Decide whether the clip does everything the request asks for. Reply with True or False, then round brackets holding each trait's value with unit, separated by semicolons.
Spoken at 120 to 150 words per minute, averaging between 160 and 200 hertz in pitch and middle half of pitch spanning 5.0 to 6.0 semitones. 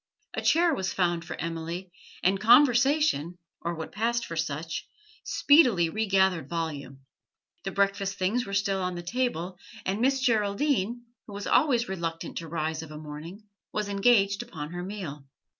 False (160 wpm; 190 Hz; 5.5 semitones)